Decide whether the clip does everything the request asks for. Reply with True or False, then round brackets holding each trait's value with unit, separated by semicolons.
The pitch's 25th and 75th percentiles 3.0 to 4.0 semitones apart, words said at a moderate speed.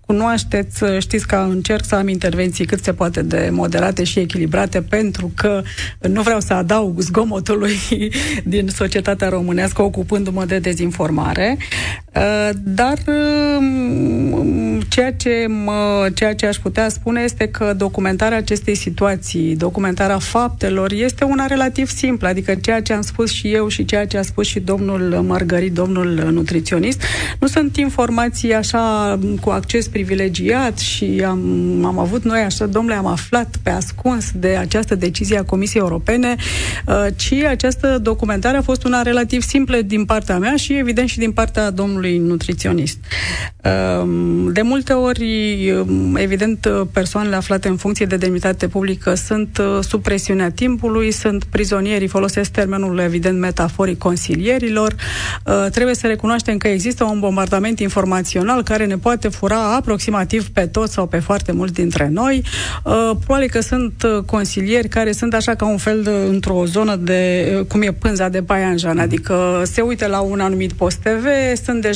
True (3.5 semitones; 150 wpm)